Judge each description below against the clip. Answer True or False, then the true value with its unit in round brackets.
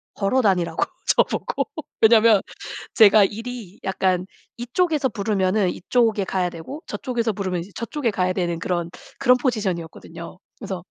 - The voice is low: False (200 Hz)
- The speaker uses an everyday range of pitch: True (4.4 semitones)